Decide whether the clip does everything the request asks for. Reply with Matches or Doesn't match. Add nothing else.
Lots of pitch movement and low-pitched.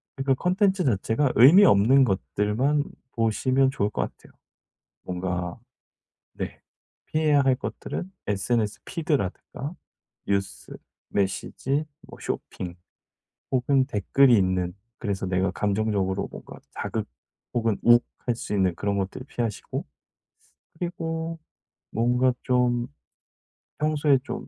Matches